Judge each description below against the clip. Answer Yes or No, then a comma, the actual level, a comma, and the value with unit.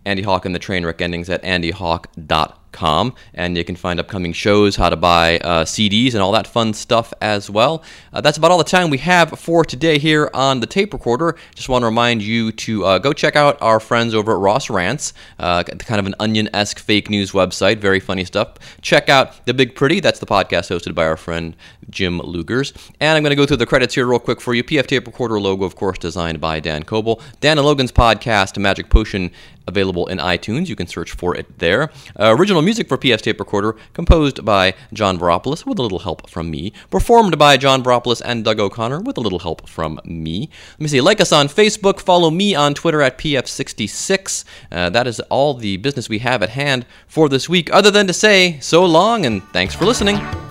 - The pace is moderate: No, fast, 220 wpm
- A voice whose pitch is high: No, low, 115 Hz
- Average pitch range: No, wide, 7.1 semitones